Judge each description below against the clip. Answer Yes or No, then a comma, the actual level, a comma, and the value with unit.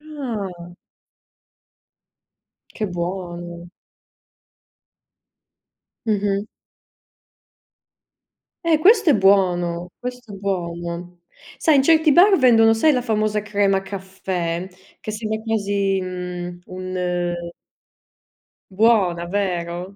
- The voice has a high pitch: Yes, high, 195 Hz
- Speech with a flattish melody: No, average, 4.0 semitones